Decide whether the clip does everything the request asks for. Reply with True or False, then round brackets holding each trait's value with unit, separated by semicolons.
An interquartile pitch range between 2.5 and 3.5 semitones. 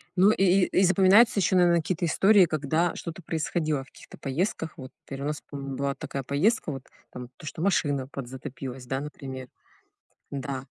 False (4.8 semitones)